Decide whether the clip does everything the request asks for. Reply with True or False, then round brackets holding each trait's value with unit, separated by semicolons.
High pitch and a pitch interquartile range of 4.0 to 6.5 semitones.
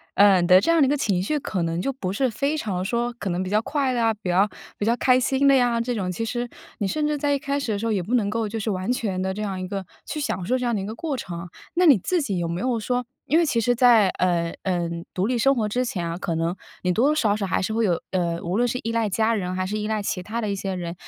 True (215 Hz; 5.0 semitones)